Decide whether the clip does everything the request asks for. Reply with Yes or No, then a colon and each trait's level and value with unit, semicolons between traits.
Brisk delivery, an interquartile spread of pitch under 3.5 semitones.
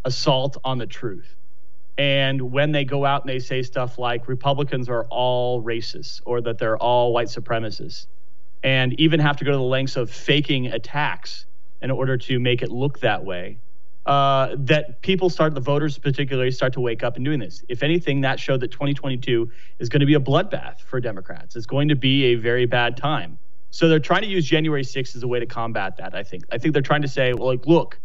Yes: fast, 220 wpm; average, 2.8 semitones